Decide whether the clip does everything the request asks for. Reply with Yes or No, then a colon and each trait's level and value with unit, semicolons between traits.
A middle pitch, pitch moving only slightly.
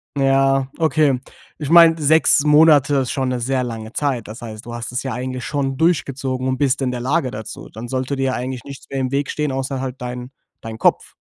No: low, 130 Hz; narrow, 2.1 semitones